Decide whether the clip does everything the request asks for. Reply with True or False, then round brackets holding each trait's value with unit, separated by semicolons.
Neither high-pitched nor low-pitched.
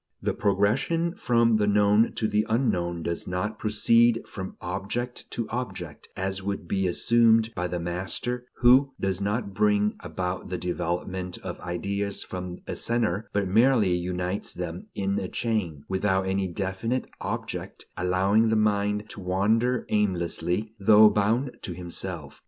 False (100 Hz)